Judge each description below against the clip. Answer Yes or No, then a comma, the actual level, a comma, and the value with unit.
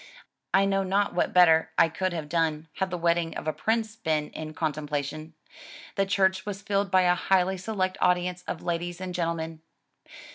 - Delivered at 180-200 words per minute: Yes, average, 185 wpm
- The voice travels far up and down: No, average, 2.9 semitones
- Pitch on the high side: No, medium, 180 Hz